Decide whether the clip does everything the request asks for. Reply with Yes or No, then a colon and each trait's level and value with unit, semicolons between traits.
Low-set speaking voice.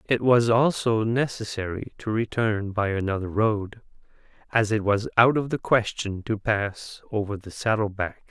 Yes: low, 110 Hz